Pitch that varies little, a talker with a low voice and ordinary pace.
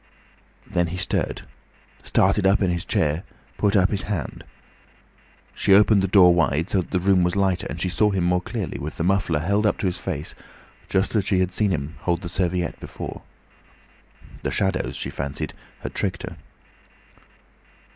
Yes: narrow, 2.2 semitones; very low, 90 Hz; average, 180 wpm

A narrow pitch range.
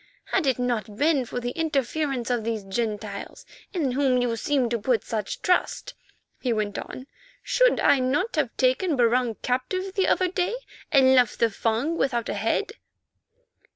No: average, 4.5 semitones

